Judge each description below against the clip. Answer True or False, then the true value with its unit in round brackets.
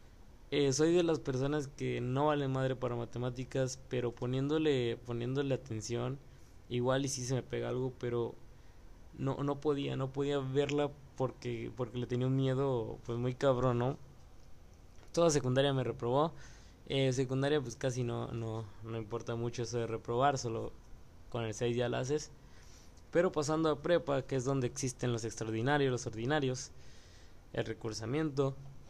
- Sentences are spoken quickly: False (160 wpm)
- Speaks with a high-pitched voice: False (125 Hz)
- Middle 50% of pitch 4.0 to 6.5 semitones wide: False (2.9 semitones)